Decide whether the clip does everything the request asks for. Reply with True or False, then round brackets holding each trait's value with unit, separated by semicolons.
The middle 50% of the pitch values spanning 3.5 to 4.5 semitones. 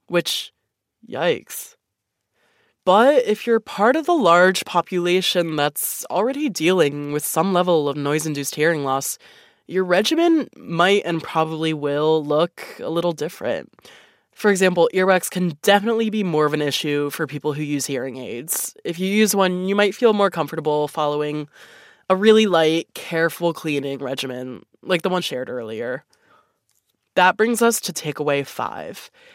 False (5.3 semitones)